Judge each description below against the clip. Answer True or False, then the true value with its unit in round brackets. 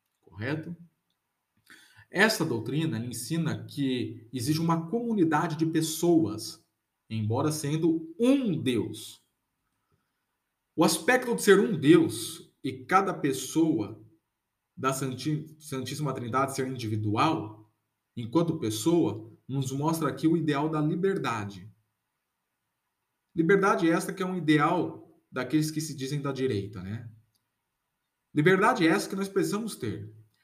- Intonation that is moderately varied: False (6.2 semitones)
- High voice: False (150 Hz)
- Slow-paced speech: True (110 wpm)